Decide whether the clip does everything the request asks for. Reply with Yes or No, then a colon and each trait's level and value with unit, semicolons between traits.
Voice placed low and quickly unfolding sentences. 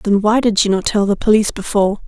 No: high, 205 Hz; fast, 260 wpm